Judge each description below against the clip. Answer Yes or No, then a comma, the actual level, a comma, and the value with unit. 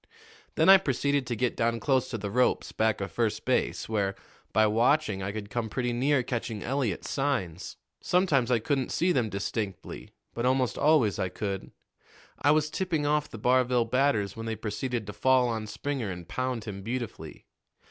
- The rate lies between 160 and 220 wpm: Yes, average, 180 wpm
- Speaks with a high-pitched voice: No, low, 120 Hz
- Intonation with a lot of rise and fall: No, average, 4.1 semitones